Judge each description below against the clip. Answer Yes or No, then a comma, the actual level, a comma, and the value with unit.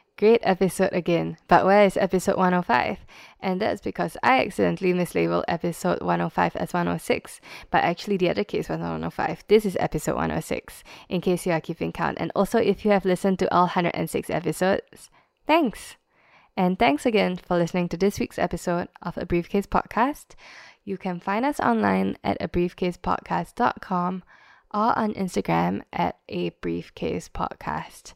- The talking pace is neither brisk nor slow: Yes, average, 160 wpm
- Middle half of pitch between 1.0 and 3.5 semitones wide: Yes, average, 2.8 semitones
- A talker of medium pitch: Yes, medium, 180 Hz